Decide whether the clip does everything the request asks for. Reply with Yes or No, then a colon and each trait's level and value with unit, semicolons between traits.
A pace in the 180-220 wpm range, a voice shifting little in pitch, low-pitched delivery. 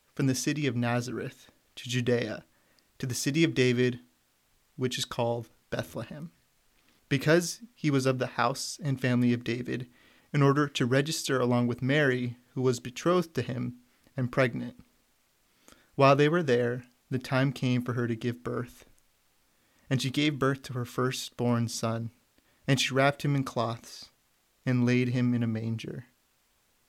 No: average, 160 wpm; narrow, 2.1 semitones; low, 125 Hz